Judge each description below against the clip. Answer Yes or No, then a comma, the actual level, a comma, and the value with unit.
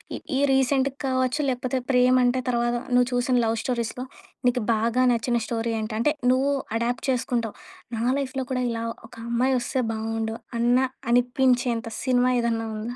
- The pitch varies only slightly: Yes, narrow, 1.8 semitones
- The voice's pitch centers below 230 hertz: No, high, 245 Hz